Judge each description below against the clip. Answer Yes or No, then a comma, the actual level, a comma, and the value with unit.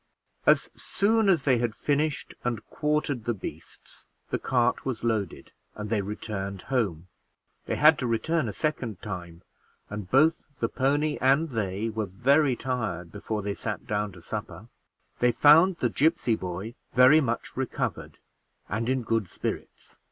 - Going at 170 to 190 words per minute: No, average, 155 wpm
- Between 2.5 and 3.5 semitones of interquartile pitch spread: No, wide, 5.4 semitones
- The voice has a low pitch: Yes, low, 120 Hz